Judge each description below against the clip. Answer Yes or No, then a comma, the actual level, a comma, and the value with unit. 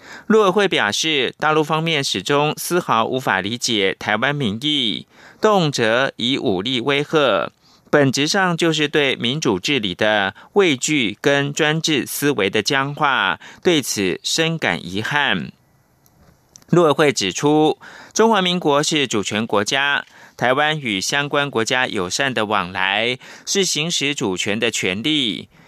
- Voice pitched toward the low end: No, medium, 145 Hz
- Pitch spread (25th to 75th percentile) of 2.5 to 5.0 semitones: No, wide, 5.5 semitones